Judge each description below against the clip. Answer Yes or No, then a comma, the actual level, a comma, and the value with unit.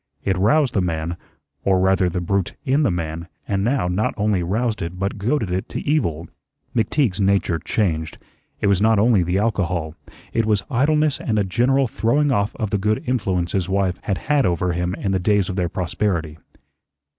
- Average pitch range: Yes, average, 4.0 semitones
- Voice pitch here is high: No, low, 100 Hz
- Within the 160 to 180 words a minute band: No, average, 190 wpm